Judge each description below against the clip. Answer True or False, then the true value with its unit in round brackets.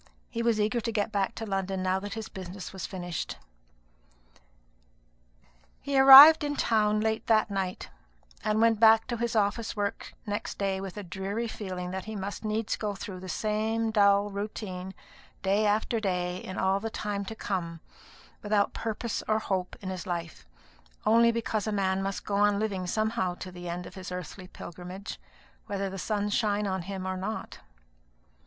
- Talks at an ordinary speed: True (175 wpm)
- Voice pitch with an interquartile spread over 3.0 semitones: False (2.6 semitones)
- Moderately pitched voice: False (205 Hz)